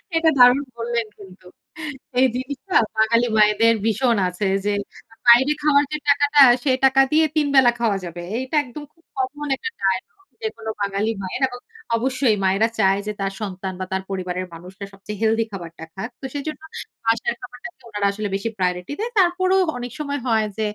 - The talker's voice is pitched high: Yes, high, 230 Hz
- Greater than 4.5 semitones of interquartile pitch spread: Yes, wide, 5.6 semitones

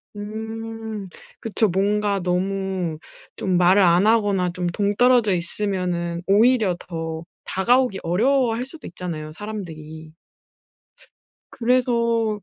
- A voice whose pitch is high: Yes, high, 200 Hz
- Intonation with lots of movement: No, average, 4.0 semitones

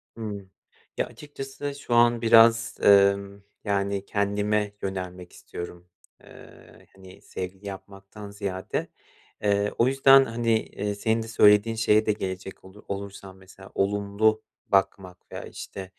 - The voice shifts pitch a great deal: No, narrow, 2.4 semitones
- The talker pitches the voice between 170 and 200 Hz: No, low, 100 Hz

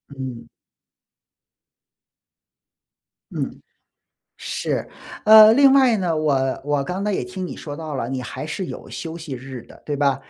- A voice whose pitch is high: No, medium, 155 Hz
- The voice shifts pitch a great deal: Yes, wide, 6.0 semitones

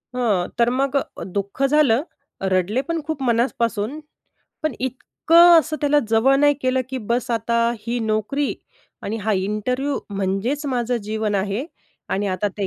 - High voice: Yes, high, 240 Hz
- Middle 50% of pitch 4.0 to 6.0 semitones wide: Yes, average, 4.5 semitones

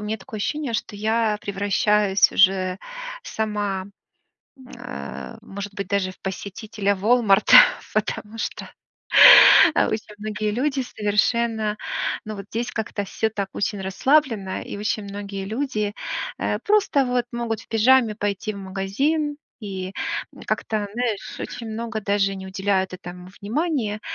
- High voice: Yes, high, 210 Hz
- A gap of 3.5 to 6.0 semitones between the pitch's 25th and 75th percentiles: No, average, 2.7 semitones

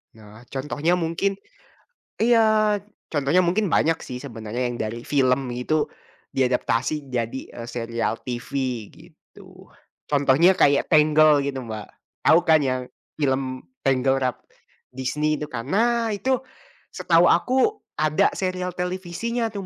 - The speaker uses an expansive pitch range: Yes, wide, 6.2 semitones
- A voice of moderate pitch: Yes, medium, 145 Hz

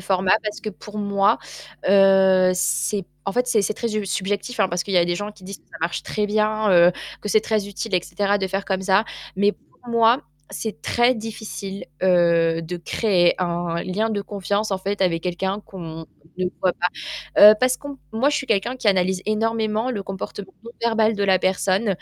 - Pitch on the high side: Yes, high, 200 Hz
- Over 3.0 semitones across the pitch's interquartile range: No, average, 2.7 semitones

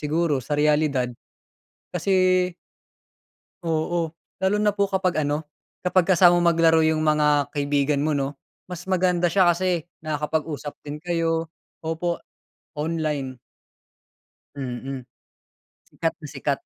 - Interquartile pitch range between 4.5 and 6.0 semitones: No, average, 3.0 semitones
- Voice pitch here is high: No, medium, 160 Hz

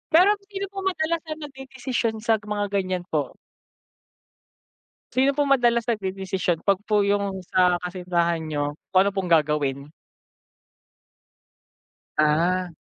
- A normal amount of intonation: No, wide, 5.7 semitones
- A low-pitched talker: No, high, 190 Hz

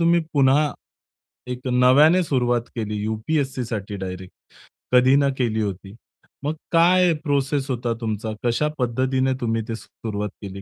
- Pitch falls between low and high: No, low, 125 Hz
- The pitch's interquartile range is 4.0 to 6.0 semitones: Yes, average, 4.3 semitones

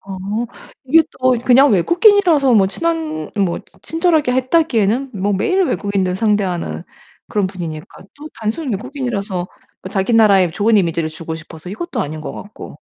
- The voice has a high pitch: Yes, high, 210 Hz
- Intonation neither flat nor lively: No, wide, 6.7 semitones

